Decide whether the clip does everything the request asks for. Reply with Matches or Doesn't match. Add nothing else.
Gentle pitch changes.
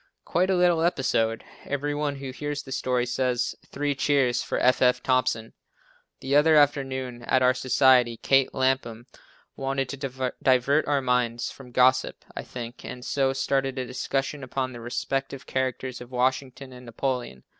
Matches